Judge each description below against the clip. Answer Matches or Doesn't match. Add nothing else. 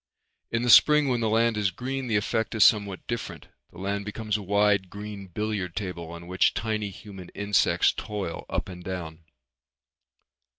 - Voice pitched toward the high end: Doesn't match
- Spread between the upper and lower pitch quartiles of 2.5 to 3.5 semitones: Matches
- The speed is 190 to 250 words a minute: Doesn't match